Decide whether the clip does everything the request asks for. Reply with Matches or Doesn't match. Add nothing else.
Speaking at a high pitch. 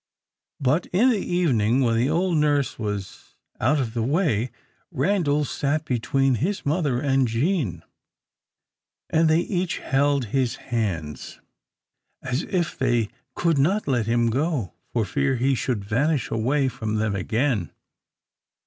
Doesn't match